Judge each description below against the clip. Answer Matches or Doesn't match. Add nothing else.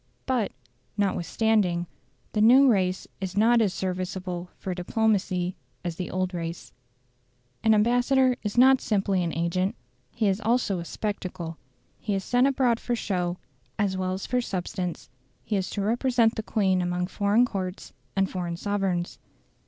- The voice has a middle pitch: Doesn't match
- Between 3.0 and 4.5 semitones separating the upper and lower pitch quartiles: Matches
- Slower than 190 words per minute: Matches